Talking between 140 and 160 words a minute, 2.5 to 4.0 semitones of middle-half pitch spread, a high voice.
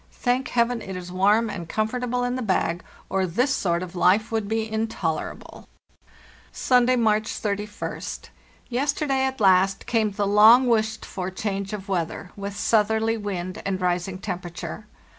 Yes: average, 150 wpm; average, 3.5 semitones; high, 210 Hz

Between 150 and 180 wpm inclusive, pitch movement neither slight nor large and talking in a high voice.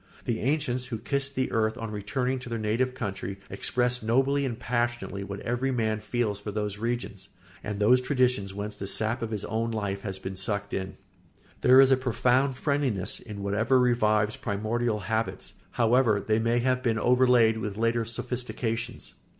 No: average, 175 wpm; average, 3.1 semitones; low, 115 Hz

